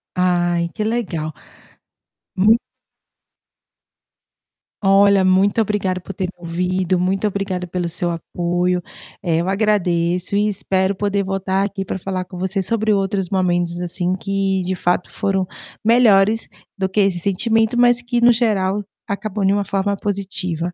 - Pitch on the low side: No, high, 190 Hz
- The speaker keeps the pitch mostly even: Yes, narrow, 2.1 semitones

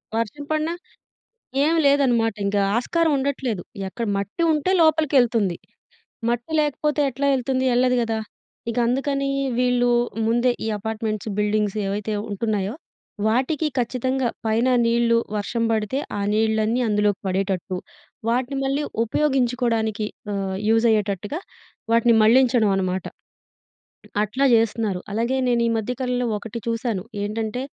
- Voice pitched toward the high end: Yes, high, 235 Hz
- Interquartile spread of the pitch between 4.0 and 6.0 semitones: No, average, 3.5 semitones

